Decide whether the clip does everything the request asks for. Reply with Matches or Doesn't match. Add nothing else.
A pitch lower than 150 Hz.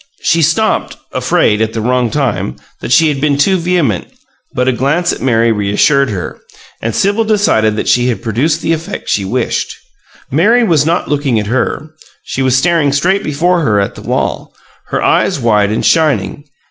Matches